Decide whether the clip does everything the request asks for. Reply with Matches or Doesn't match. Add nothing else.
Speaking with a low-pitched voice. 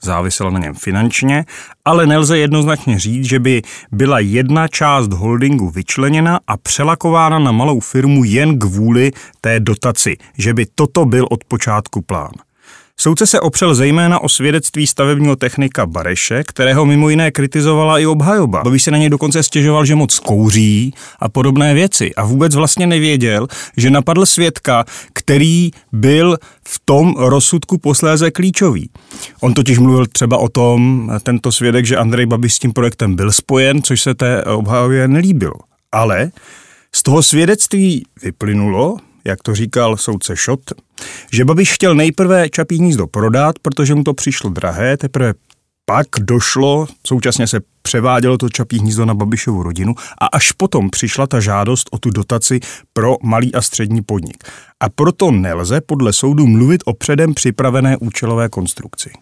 Matches